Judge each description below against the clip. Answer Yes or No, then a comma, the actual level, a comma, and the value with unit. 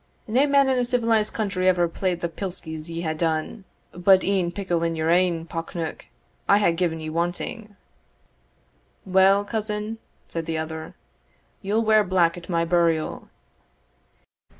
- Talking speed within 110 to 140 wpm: No, average, 150 wpm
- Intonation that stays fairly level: No, average, 3.8 semitones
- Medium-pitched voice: Yes, medium, 180 Hz